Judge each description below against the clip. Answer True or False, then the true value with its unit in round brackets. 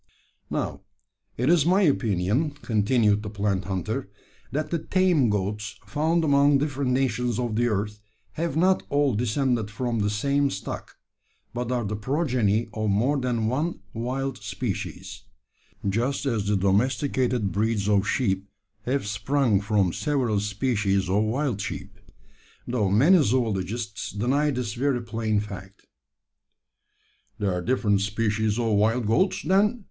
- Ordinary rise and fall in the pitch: True (4.8 semitones)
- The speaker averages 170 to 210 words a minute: False (140 wpm)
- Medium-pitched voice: False (115 Hz)